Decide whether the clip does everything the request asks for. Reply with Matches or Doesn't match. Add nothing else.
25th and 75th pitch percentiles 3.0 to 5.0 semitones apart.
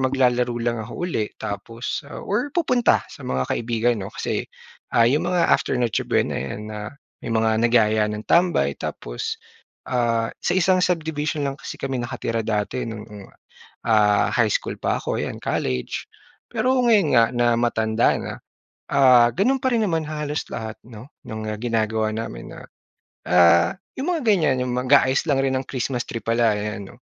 Doesn't match